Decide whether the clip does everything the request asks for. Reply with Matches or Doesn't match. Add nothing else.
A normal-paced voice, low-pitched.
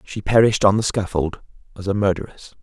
Matches